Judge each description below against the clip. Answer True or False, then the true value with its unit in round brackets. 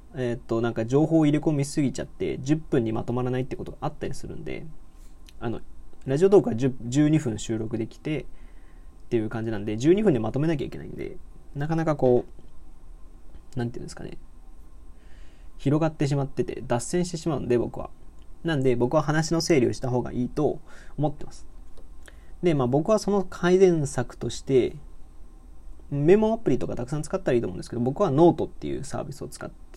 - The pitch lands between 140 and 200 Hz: False (125 Hz)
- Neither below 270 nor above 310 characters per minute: False (385 characters per minute)